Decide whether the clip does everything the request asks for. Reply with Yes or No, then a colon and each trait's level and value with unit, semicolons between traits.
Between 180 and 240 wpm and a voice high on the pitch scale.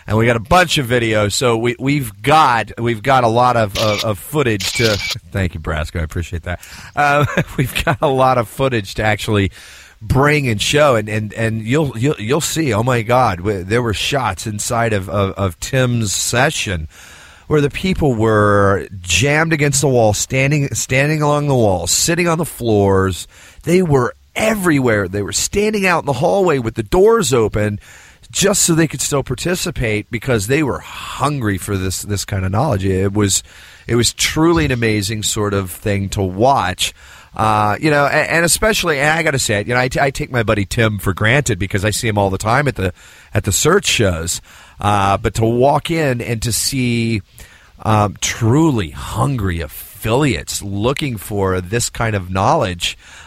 No: average, 195 wpm; low, 115 Hz